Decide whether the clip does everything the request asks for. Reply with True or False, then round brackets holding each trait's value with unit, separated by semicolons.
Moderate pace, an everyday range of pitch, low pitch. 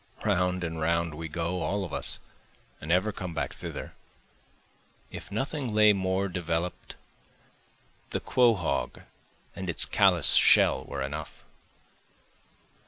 False (120 wpm; 3.2 semitones; 90 Hz)